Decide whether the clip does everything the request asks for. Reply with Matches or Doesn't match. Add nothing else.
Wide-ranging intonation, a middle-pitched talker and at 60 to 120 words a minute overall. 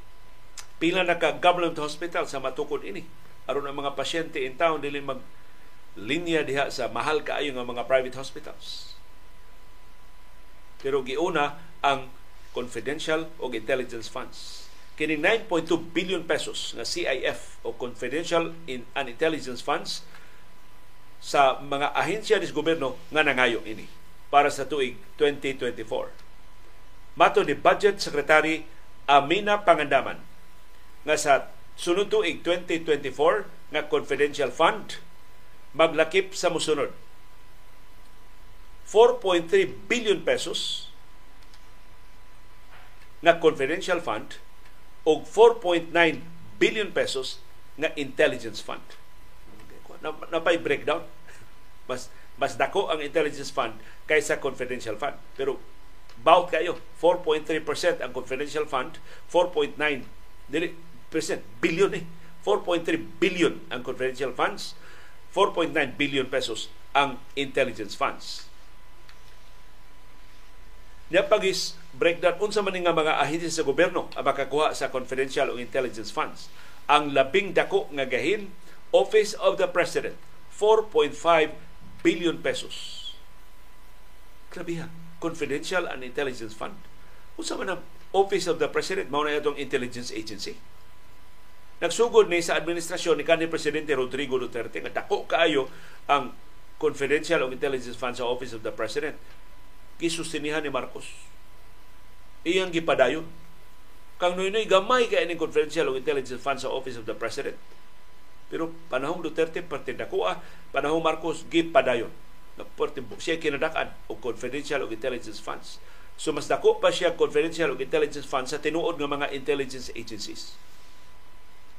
Matches